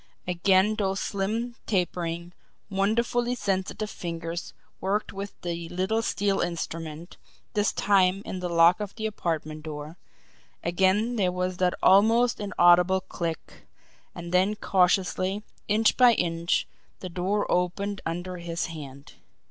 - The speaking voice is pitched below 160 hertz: No, medium, 185 Hz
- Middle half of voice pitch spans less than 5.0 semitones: Yes, average, 3.0 semitones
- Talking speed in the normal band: No, slow, 125 wpm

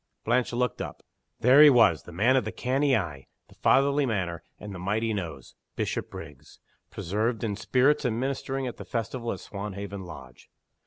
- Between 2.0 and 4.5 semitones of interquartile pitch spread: No, wide, 5.4 semitones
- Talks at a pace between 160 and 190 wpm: Yes, average, 170 wpm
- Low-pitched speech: Yes, low, 110 Hz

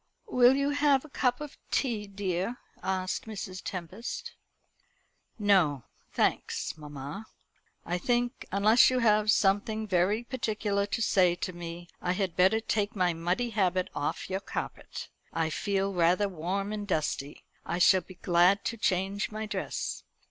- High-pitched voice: Yes, high, 195 Hz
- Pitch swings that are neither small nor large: Yes, average, 3.5 semitones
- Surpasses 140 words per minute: Yes, average, 150 wpm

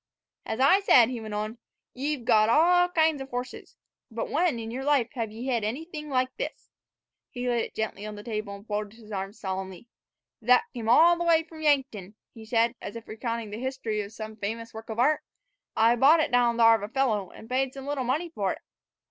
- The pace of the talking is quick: Yes, fast, 225 wpm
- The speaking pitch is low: No, high, 235 Hz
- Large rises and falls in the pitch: No, average, 3.8 semitones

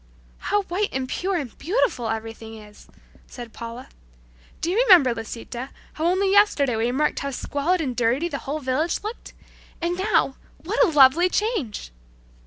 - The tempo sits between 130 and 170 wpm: Yes, average, 160 wpm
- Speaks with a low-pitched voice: No, very high, 285 Hz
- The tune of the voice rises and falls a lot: Yes, wide, 7.1 semitones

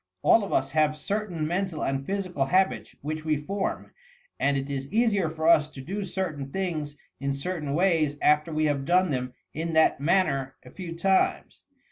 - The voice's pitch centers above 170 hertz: No, medium, 155 Hz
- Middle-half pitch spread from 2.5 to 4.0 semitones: No, average, 4.6 semitones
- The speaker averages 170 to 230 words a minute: Yes, average, 180 wpm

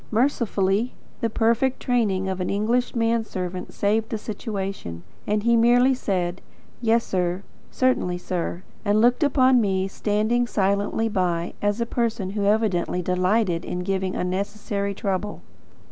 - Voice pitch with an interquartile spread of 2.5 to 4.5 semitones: Yes, average, 3.6 semitones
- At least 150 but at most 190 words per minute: No, slow, 135 wpm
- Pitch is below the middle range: No, high, 205 Hz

